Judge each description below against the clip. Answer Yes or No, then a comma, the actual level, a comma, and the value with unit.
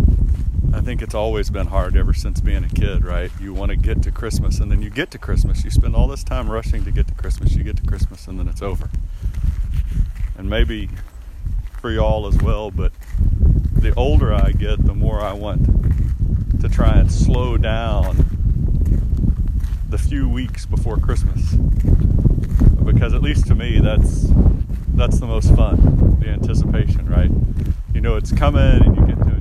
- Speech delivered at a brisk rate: No, average, 180 wpm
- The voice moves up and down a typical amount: Yes, average, 3.9 semitones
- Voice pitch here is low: Yes, very low, 90 Hz